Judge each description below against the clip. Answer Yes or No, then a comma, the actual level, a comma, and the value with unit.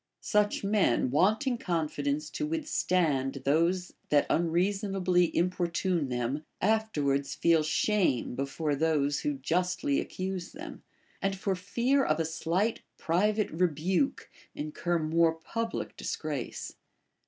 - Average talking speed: No, slow, 110 wpm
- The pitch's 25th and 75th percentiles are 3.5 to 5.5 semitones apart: Yes, average, 4.6 semitones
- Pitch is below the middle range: No, medium, 175 Hz